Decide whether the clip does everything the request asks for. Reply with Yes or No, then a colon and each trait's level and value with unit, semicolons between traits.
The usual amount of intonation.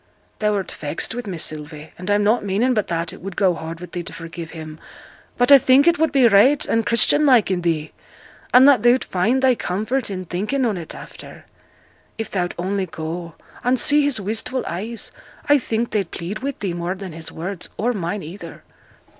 No: wide, 6.0 semitones